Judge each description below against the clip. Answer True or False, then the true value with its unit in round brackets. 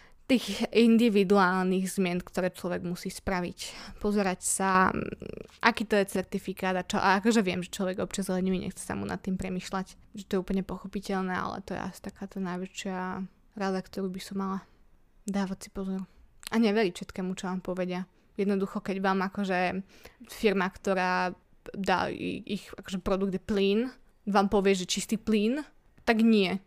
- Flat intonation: True (1.6 semitones)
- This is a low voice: False (195 Hz)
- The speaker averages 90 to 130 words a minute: False (160 wpm)